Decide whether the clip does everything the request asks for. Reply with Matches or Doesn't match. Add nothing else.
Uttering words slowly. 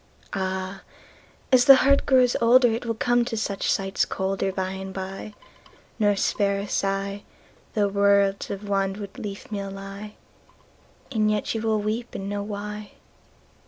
Matches